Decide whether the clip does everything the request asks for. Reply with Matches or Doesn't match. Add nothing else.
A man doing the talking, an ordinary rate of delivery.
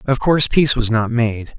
Doesn't match